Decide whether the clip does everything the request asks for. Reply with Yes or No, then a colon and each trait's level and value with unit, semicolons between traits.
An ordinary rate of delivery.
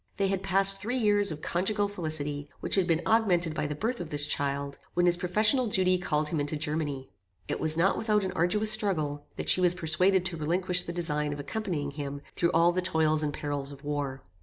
No: fast, 215 wpm